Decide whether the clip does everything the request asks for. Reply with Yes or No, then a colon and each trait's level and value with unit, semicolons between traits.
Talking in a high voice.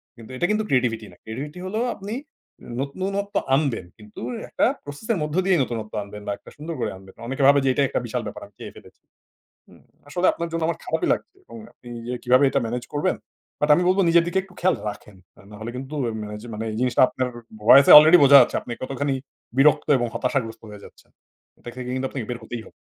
No: low, 135 Hz